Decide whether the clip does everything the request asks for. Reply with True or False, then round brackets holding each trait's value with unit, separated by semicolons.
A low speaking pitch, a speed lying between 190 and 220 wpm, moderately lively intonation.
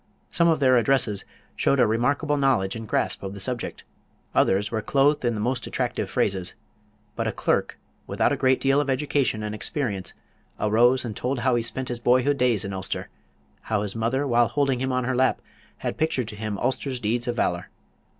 True (120 Hz; 200 wpm; 3.8 semitones)